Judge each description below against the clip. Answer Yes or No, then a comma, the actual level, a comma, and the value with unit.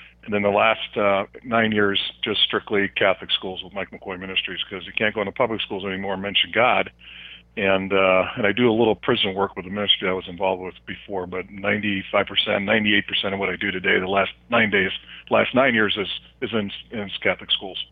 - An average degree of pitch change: No, narrow, 1.5 semitones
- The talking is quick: Yes, fast, 215 wpm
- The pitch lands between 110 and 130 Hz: No, low, 100 Hz